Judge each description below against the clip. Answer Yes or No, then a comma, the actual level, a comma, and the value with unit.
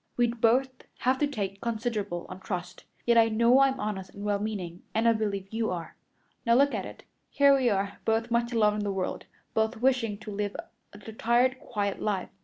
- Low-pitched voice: No, high, 220 Hz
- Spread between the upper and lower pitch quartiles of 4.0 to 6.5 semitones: No, average, 2.9 semitones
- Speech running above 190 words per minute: Yes, fast, 205 wpm